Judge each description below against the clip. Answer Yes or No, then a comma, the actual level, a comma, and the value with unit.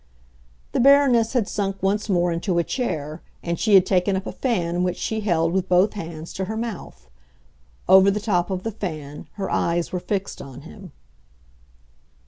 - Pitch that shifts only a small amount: No, average, 3.6 semitones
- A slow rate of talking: No, average, 180 wpm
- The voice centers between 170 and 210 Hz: Yes, high, 190 Hz